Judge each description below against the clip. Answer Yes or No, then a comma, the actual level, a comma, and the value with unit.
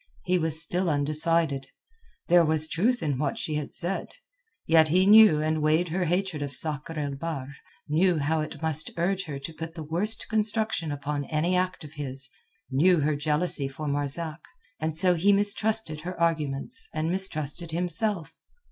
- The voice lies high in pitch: No, medium, 160 Hz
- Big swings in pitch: No, average, 3.2 semitones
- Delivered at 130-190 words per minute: Yes, average, 170 wpm